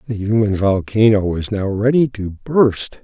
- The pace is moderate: Yes, average, 160 wpm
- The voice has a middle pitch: No, low, 105 Hz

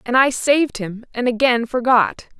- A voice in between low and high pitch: No, high, 245 Hz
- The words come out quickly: No, average, 150 wpm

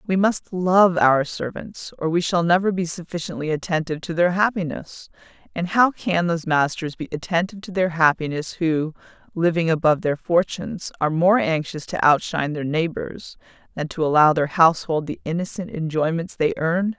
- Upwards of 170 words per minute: No, average, 165 wpm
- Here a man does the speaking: No, female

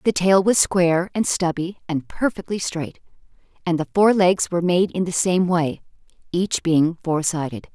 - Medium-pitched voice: Yes, medium, 175 Hz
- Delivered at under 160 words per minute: No, average, 180 wpm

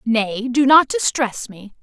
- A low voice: No, very high, 250 Hz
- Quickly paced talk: No, average, 165 wpm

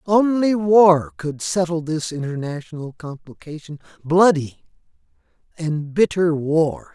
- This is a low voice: No, medium, 165 Hz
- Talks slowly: Yes, slow, 85 wpm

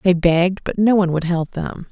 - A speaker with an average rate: No, fast, 250 wpm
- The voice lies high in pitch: No, medium, 180 Hz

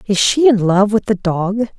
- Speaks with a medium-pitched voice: No, high, 210 Hz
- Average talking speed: No, fast, 235 wpm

